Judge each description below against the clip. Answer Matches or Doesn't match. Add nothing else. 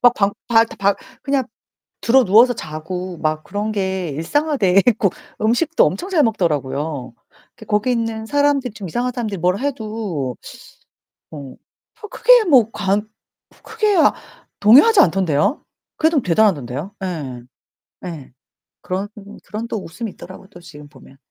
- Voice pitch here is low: Doesn't match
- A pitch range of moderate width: Doesn't match